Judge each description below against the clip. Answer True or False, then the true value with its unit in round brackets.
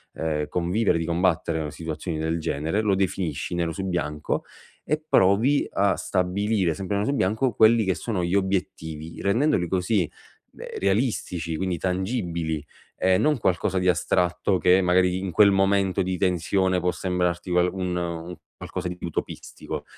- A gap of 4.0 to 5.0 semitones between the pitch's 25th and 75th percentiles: False (2.5 semitones)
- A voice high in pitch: False (90 Hz)